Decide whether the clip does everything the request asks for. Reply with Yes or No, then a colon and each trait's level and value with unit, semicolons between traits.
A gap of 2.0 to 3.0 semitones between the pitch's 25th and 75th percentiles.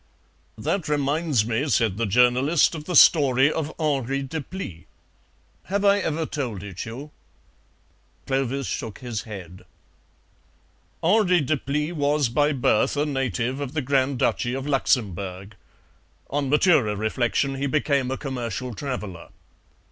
No: average, 4.3 semitones